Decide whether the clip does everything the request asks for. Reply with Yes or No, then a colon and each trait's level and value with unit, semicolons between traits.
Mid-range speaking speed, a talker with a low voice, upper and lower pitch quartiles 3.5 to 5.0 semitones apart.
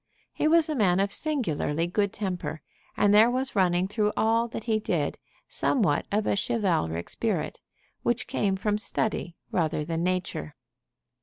No: average, 155 wpm; high, 200 Hz; average, 4.4 semitones